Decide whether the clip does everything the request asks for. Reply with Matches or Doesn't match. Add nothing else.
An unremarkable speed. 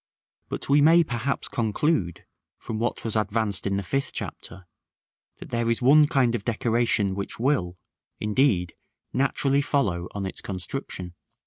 Matches